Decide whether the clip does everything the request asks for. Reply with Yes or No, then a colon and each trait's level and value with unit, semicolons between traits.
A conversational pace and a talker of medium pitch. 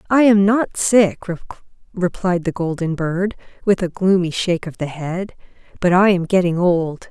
Yes: average, 170 wpm; medium, 180 Hz